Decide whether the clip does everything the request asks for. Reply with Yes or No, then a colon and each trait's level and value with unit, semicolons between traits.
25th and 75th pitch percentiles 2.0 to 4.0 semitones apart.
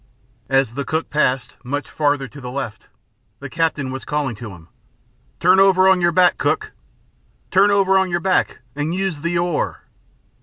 No: wide, 5.5 semitones